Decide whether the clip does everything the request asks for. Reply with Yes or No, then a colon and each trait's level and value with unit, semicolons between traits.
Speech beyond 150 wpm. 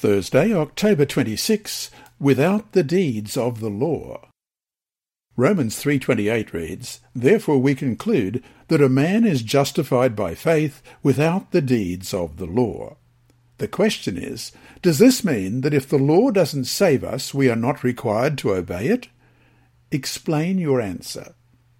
No: average, 140 wpm